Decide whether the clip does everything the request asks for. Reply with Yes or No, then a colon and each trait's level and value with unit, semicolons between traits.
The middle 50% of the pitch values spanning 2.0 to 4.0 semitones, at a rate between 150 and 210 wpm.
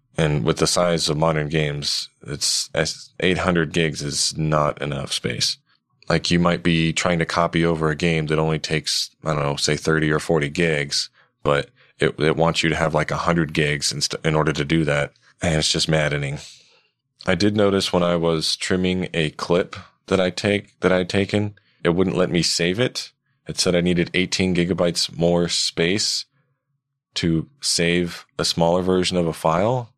Yes: average, 2.8 semitones; average, 185 wpm